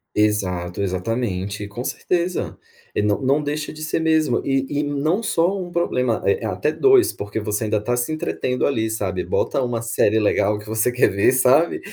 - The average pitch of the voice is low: Yes, low, 125 Hz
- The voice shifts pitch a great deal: Yes, wide, 6.5 semitones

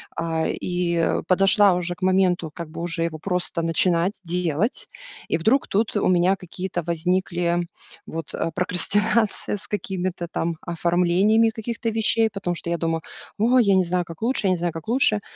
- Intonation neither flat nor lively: Yes, average, 3.1 semitones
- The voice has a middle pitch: Yes, medium, 180 Hz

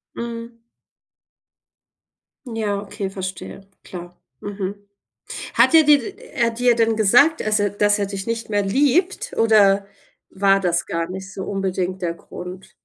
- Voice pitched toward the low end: No, high, 205 Hz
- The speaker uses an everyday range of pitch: Yes, average, 3.2 semitones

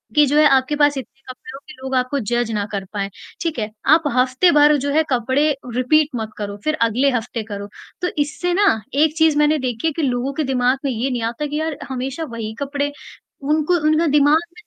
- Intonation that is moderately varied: Yes, average, 3.7 semitones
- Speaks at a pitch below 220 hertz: No, very high, 270 Hz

